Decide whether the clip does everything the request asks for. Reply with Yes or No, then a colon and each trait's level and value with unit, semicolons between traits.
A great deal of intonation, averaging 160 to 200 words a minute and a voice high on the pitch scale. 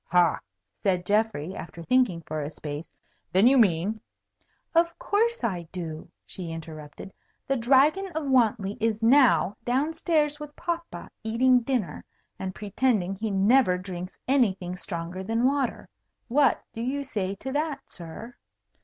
No: wide, 6.9 semitones; average, 145 wpm; high, 220 Hz